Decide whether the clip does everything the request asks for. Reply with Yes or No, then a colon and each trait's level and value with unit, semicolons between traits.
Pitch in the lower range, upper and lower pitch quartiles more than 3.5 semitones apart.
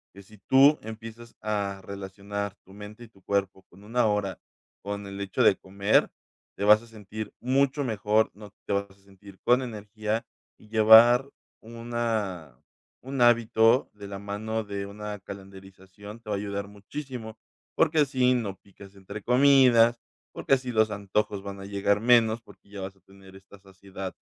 No: low, 105 Hz; narrow, 2.6 semitones